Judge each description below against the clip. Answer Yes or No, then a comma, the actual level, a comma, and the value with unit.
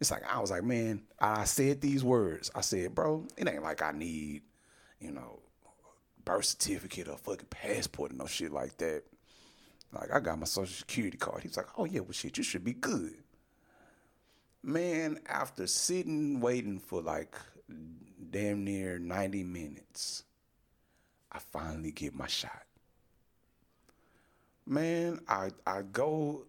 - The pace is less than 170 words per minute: Yes, average, 150 wpm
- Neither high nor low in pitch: No, low, 100 Hz